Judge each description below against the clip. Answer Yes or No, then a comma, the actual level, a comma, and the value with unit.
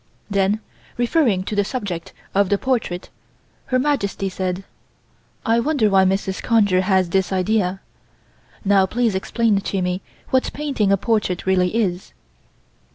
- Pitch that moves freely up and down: No, average, 3.3 semitones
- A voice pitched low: No, high, 200 Hz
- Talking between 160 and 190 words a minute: No, average, 140 wpm